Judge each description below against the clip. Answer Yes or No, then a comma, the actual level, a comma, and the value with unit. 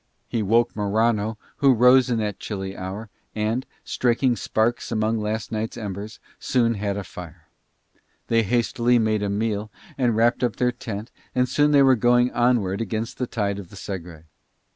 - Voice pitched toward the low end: Yes, low, 110 Hz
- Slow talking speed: No, average, 170 wpm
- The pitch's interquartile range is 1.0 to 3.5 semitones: Yes, average, 2.8 semitones